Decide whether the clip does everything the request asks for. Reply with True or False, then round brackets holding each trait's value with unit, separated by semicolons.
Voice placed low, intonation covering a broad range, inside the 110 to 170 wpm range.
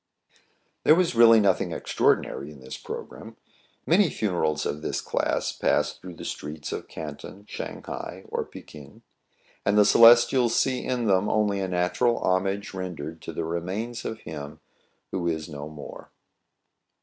True (95 Hz; 6.3 semitones; 155 wpm)